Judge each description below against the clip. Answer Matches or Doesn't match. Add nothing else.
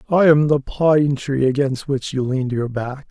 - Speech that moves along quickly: Matches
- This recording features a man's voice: Matches